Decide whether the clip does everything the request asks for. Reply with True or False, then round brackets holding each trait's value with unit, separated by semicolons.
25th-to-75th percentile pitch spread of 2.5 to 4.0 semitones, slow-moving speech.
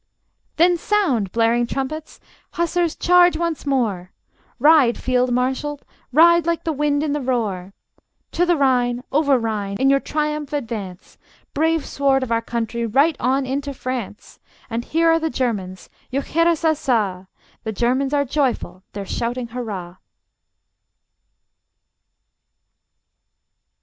False (4.8 semitones; 125 wpm)